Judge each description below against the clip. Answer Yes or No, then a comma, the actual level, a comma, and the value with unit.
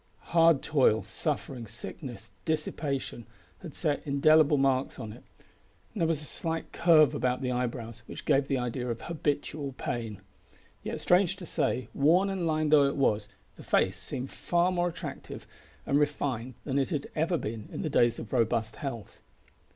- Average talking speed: Yes, average, 170 wpm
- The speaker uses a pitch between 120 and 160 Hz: Yes, medium, 140 Hz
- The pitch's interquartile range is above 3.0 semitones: Yes, average, 4.4 semitones